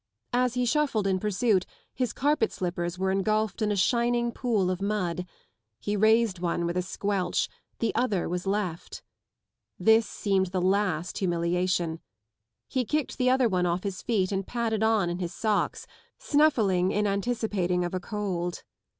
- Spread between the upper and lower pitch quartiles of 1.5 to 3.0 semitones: No, average, 3.8 semitones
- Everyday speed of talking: Yes, average, 160 wpm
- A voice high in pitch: Yes, high, 200 Hz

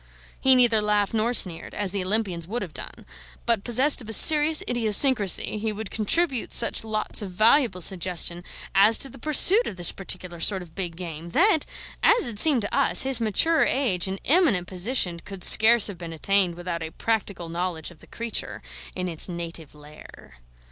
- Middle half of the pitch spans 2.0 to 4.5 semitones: No, average, 5.2 semitones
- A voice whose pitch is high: Yes, high, 205 Hz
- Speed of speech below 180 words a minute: No, average, 185 wpm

